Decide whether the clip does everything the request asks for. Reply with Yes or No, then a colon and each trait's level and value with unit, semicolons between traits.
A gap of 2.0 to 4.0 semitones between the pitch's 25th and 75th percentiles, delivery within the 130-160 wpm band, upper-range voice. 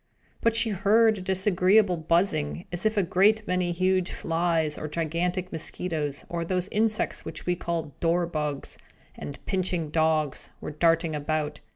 No: average, 3.1 semitones; average, 155 wpm; medium, 175 Hz